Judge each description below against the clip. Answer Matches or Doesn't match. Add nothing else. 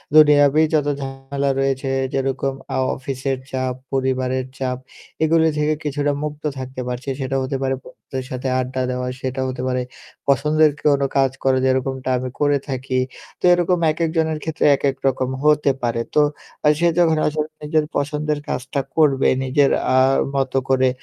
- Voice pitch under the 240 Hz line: Matches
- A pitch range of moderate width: Doesn't match